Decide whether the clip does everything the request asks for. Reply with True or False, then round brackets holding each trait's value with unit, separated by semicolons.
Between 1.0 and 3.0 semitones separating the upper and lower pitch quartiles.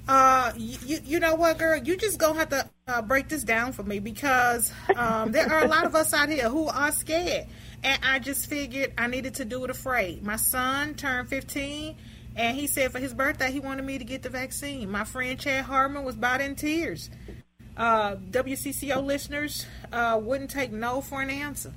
True (2.4 semitones)